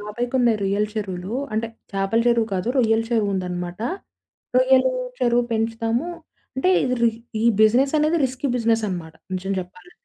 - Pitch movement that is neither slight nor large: Yes, average, 4.0 semitones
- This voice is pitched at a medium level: No, high, 225 Hz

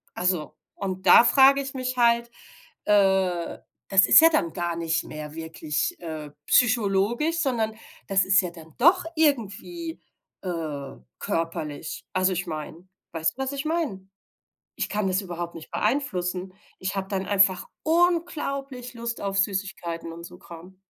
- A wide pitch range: Yes, wide, 6.5 semitones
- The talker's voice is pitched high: Yes, high, 195 Hz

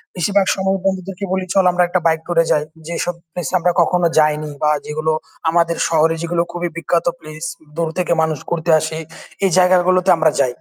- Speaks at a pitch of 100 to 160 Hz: No, medium, 170 Hz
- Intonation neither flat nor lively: No, narrow, 2.3 semitones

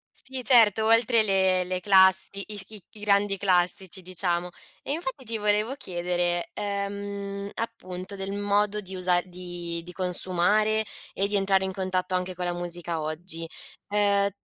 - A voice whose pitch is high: Yes, high, 195 Hz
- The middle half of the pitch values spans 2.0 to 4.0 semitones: Yes, narrow, 2.4 semitones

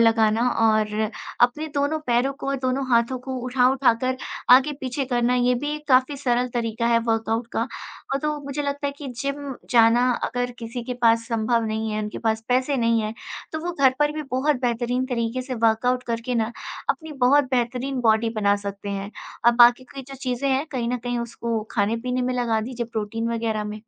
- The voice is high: Yes, high, 245 Hz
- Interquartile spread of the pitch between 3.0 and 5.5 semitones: No, narrow, 2.5 semitones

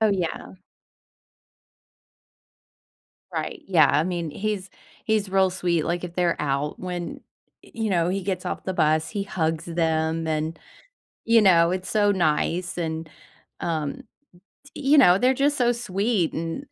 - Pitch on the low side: No, medium, 180 Hz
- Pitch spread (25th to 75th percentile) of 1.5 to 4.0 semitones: Yes, average, 3.6 semitones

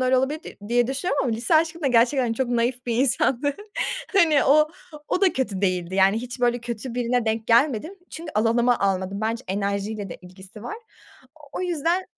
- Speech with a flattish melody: No, average, 4.2 semitones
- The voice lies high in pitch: Yes, high, 245 Hz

